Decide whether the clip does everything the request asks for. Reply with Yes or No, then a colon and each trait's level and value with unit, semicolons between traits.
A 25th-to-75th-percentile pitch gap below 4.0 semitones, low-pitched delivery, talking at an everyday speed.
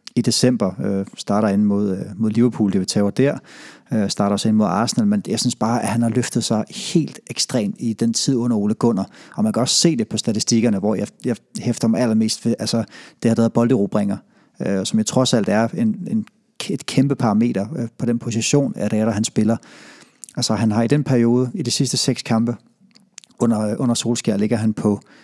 No: average, 3.4 semitones; low, 120 Hz; fast, 230 wpm